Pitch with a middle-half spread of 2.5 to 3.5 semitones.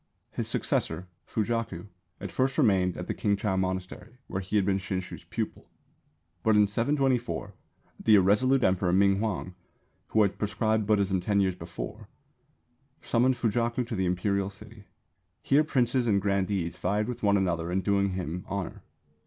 Yes: average, 3.0 semitones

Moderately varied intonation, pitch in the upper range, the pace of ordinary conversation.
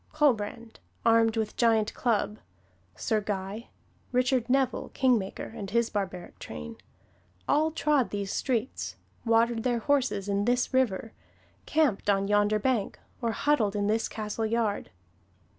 No: average, 3.3 semitones; high, 225 Hz; slow, 130 wpm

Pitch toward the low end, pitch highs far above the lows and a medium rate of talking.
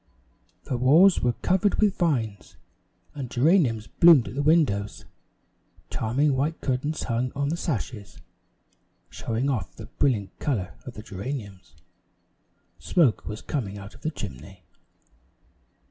No: low, 130 Hz; wide, 6.0 semitones; slow, 130 wpm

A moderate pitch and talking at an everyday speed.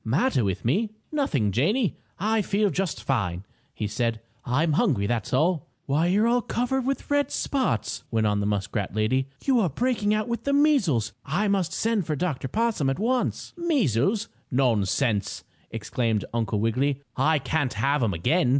Yes: medium, 150 Hz; average, 170 wpm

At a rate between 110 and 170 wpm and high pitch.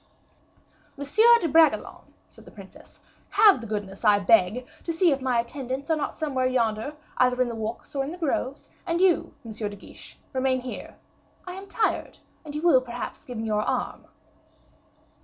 No: average, 180 wpm; very high, 260 Hz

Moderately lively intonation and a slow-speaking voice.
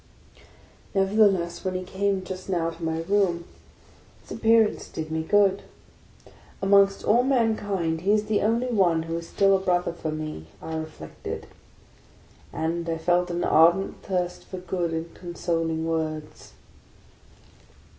No: average, 3.2 semitones; average, 145 wpm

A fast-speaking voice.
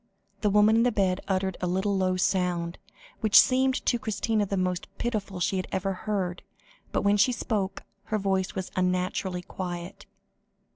No: average, 165 wpm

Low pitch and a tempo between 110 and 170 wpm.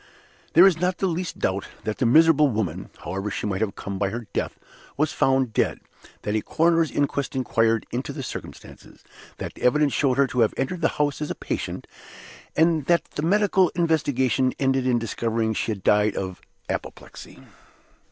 No: low, 130 Hz; average, 185 wpm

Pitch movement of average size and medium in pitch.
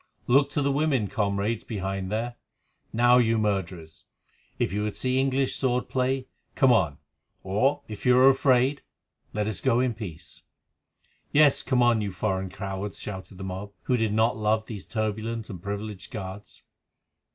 No: average, 4.4 semitones; low, 110 Hz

